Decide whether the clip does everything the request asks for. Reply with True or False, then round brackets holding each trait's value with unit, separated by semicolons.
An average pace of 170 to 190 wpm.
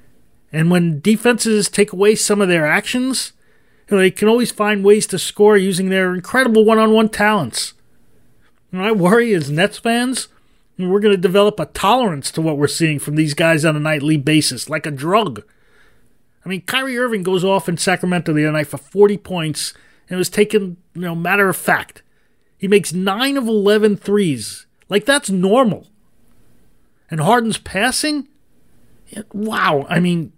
True (180 wpm)